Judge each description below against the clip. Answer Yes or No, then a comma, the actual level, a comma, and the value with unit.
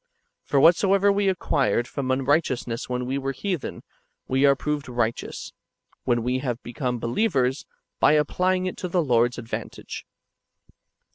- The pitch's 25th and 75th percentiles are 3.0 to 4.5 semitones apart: No, average, 5.3 semitones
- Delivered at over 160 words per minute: No, average, 150 wpm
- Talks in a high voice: No, low, 135 Hz